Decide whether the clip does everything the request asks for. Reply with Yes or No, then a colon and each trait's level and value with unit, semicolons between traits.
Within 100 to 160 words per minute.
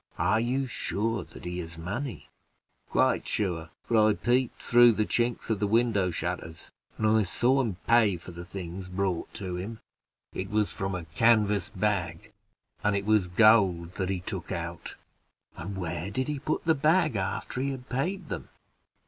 No: average, 175 wpm